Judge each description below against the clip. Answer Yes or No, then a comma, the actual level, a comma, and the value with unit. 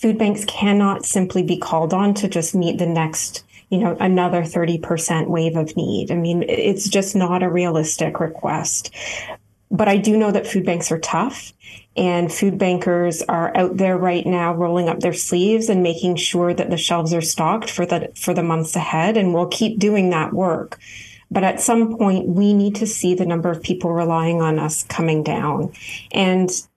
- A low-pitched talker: No, medium, 175 Hz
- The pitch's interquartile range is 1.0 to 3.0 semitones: Yes, narrow, 2.6 semitones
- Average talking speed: Yes, average, 195 wpm